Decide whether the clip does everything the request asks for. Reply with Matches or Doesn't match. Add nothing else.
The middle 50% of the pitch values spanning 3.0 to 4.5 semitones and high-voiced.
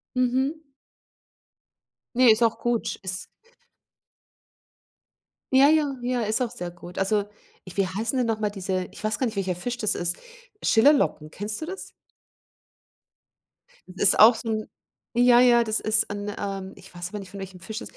Matches